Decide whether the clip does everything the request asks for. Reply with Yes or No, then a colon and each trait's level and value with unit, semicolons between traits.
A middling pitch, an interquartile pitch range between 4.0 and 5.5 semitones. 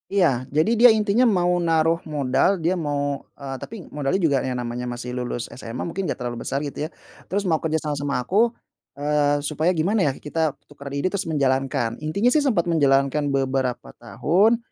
Yes: medium, 150 Hz; average, 4.8 semitones